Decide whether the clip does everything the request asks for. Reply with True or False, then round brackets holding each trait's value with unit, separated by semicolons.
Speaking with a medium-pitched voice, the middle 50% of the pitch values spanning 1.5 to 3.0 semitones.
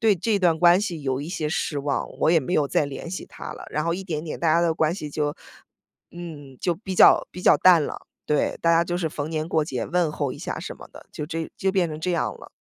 True (165 Hz; 2.7 semitones)